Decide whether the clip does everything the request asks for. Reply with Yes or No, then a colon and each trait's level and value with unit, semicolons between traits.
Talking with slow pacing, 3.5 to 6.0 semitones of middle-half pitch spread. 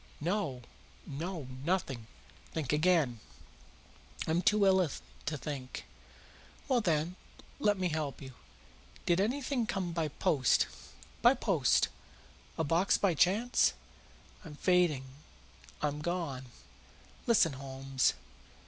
Yes: slow, 105 wpm; average, 5.0 semitones